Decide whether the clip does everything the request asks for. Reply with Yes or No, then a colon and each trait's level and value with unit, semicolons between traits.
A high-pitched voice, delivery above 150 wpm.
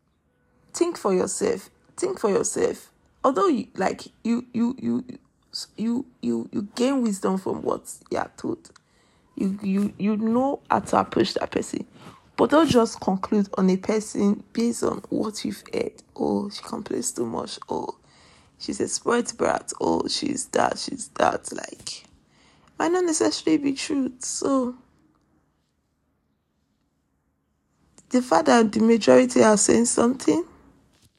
No: high, 225 Hz; average, 140 wpm